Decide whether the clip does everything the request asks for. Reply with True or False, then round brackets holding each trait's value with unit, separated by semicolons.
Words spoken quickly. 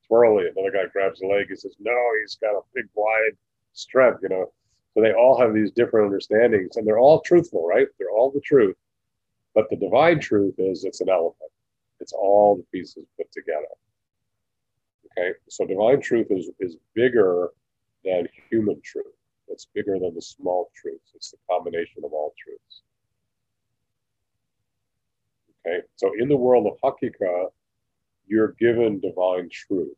False (160 wpm)